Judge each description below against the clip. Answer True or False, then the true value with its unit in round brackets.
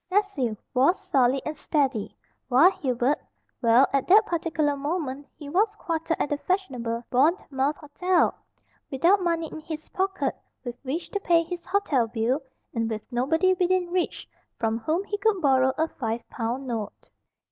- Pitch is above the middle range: True (295 Hz)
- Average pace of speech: True (160 wpm)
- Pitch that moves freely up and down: True (5.7 semitones)